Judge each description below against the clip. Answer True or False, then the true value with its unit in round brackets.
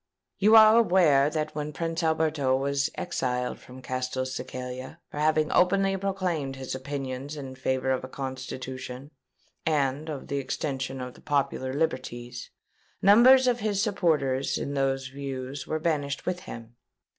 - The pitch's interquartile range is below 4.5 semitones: True (3.7 semitones)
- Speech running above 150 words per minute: False (145 wpm)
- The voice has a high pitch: False (140 Hz)